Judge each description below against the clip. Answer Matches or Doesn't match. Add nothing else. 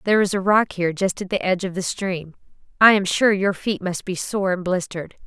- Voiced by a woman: Matches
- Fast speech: Matches